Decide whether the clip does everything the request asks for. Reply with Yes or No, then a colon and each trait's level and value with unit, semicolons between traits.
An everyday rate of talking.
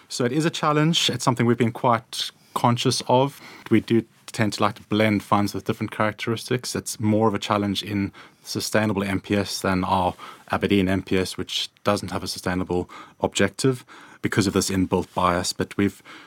Yes: average, 175 wpm